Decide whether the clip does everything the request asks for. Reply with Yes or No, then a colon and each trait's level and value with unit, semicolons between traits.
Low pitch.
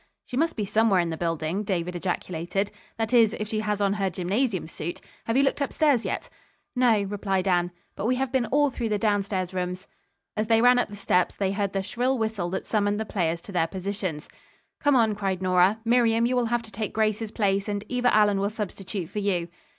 No: high, 205 Hz